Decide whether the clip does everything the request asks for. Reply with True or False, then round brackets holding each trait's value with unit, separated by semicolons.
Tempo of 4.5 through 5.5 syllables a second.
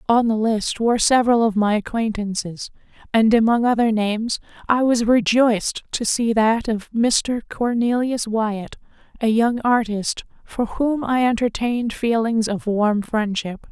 False (4.3 syllables/s)